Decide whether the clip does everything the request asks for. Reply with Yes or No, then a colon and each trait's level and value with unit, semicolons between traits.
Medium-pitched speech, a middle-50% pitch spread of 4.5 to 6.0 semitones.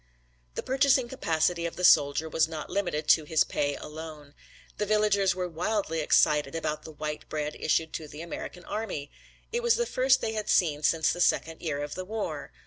Yes: medium, 165 Hz; wide, 5.4 semitones